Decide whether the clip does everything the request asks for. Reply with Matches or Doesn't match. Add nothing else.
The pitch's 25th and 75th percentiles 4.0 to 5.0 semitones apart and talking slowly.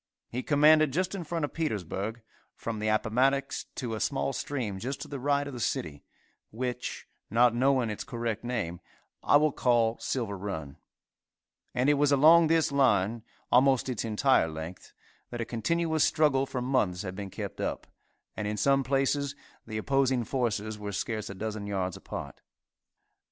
Doesn't match